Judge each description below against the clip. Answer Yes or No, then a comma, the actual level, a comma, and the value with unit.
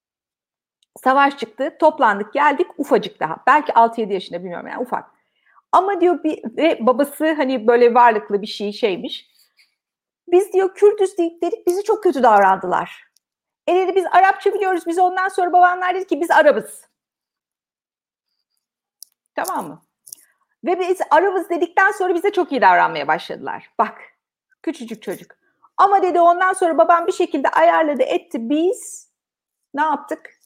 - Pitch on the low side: No, very high, 340 Hz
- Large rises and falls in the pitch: Yes, wide, 5.9 semitones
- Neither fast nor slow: No, fast, 145 wpm